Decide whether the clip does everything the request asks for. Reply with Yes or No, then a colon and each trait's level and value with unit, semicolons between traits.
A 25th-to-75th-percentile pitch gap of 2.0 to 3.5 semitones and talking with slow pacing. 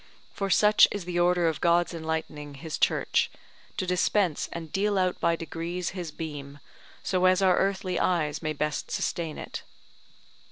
No: narrow, 2.5 semitones; average, 160 wpm